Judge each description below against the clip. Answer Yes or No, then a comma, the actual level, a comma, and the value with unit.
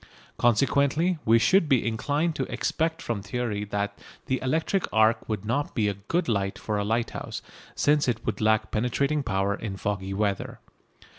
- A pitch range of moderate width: No, wide, 5.7 semitones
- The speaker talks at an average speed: Yes, average, 165 wpm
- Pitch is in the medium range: No, low, 115 Hz